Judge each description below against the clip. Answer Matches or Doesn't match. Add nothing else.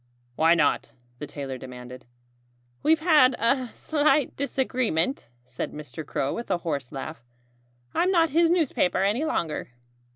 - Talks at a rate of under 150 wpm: Matches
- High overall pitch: Matches